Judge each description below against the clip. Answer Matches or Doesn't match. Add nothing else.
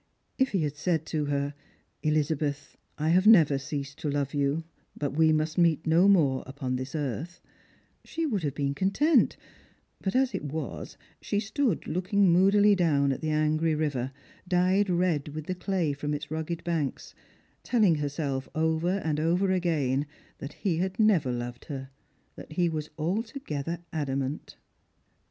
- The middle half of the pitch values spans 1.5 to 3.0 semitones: Doesn't match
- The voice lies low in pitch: Doesn't match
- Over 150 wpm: Matches